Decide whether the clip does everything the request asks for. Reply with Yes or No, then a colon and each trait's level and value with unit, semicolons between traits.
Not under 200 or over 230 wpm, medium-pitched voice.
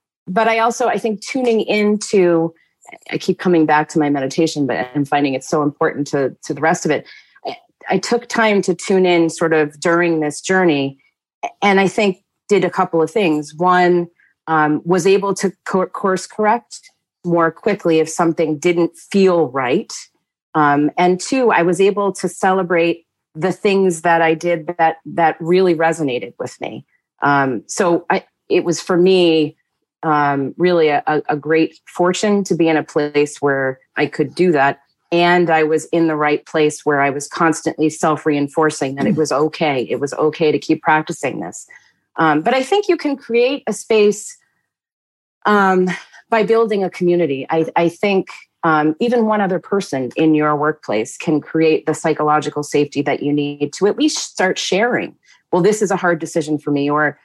No: average, 180 wpm; medium, 165 Hz